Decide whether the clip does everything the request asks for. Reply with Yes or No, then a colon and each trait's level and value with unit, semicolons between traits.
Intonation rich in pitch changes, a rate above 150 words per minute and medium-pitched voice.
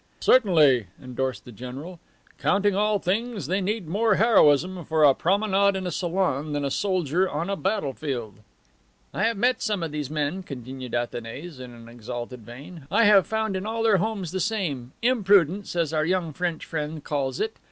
Yes: wide, 6.4 semitones; average, 180 wpm; medium, 170 Hz